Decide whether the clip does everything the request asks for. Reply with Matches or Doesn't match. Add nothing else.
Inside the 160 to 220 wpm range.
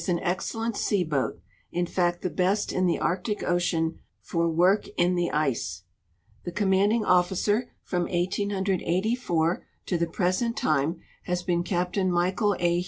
Doesn't match